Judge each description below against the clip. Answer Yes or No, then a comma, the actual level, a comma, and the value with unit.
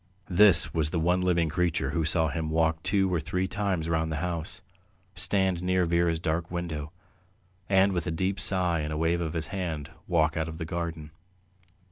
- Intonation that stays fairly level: Yes, narrow, 2.2 semitones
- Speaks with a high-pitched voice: No, very low, 85 Hz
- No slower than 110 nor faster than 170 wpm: No, average, 190 wpm